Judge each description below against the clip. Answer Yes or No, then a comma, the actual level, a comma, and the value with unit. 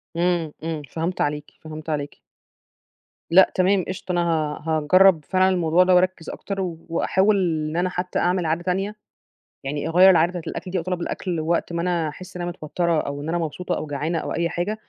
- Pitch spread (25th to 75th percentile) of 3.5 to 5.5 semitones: No, narrow, 2.5 semitones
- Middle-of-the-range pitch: Yes, medium, 175 Hz